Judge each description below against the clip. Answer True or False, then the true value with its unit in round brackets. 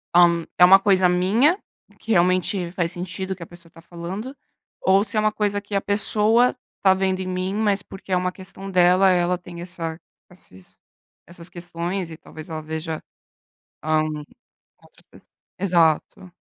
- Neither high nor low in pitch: True (180 Hz)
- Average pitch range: False (2.3 semitones)